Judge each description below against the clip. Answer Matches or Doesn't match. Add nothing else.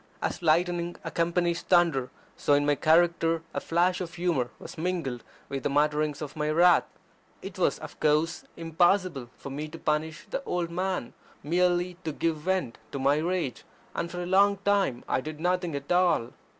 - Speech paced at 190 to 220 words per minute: Doesn't match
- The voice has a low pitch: Doesn't match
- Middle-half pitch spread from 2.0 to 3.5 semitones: Matches